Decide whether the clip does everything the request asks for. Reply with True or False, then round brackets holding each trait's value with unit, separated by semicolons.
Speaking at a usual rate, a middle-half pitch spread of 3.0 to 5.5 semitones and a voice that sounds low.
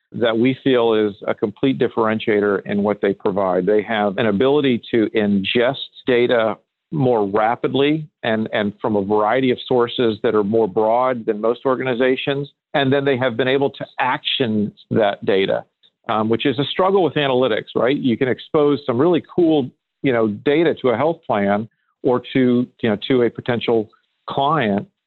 True (175 wpm; 3.7 semitones; 120 Hz)